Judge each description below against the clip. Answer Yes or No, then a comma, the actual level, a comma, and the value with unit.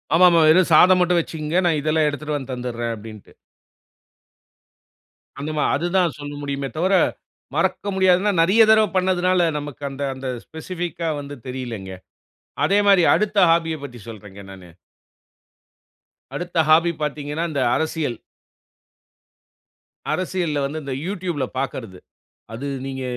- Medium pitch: Yes, medium, 155 Hz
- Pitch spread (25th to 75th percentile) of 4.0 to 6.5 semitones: Yes, average, 4.6 semitones